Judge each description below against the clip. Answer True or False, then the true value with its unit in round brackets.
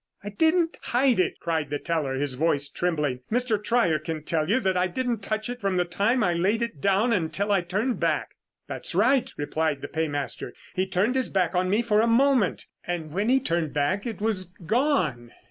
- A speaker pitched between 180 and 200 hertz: True (190 Hz)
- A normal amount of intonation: False (6.3 semitones)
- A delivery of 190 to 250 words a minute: True (205 wpm)